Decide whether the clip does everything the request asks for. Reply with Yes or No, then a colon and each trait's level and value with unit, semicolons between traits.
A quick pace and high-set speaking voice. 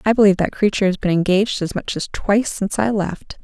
Yes: fast, 245 wpm; high, 200 Hz